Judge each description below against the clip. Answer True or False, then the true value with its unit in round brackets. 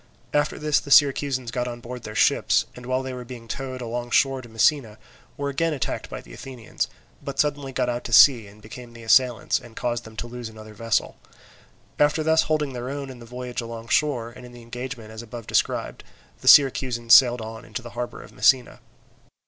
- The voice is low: True (125 Hz)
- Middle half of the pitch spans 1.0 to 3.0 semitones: True (2.5 semitones)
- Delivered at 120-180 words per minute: False (205 wpm)